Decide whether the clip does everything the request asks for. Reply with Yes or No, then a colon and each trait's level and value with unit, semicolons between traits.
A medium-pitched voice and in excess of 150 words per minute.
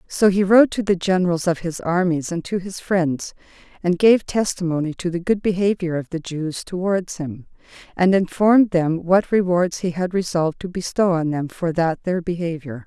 Yes: medium, 175 Hz; average, 190 wpm